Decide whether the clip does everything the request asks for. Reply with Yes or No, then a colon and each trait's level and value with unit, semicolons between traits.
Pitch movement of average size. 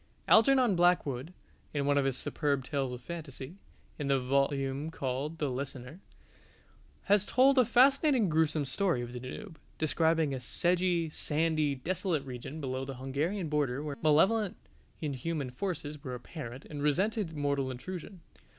Yes: average, 4.5 semitones